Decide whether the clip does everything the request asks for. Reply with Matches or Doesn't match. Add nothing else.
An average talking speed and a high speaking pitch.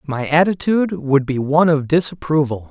Doesn't match